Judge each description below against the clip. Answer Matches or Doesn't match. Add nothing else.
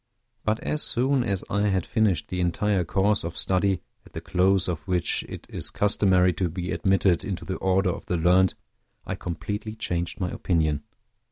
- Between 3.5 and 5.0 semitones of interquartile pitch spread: Doesn't match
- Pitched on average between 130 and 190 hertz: Doesn't match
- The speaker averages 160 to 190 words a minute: Matches